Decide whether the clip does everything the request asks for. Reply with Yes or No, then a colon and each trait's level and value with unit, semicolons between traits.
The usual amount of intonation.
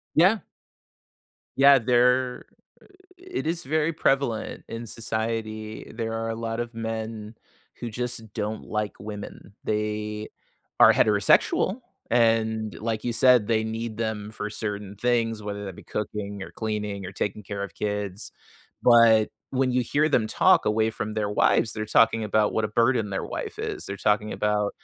No: narrow, 1.8 semitones